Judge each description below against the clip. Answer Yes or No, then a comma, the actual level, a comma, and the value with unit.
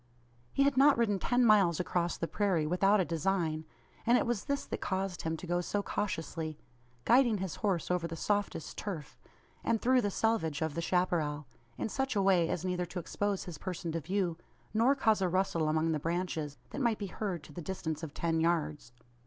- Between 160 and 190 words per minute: No, fast, 205 wpm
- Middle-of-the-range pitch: Yes, medium, 180 Hz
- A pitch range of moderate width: Yes, average, 4.1 semitones